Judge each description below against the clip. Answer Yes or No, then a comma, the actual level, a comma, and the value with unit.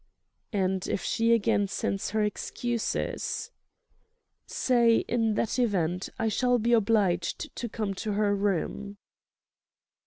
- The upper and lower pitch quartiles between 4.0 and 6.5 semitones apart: No, average, 2.7 semitones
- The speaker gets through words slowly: Yes, slow, 120 wpm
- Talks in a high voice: Yes, high, 210 Hz